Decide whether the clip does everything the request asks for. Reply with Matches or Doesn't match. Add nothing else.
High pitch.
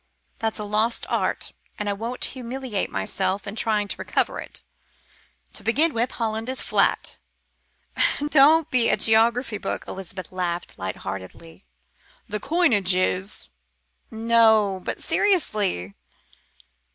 Matches